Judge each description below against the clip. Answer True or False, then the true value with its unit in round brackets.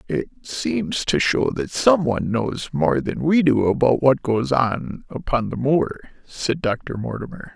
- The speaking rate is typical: True (165 wpm)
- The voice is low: True (130 Hz)